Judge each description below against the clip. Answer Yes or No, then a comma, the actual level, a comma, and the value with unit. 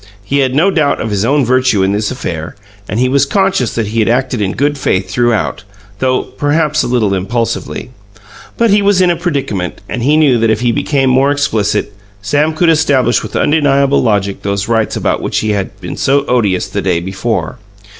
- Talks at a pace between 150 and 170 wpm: No, fast, 205 wpm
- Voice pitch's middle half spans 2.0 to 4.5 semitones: No, wide, 5.5 semitones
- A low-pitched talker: Yes, low, 125 Hz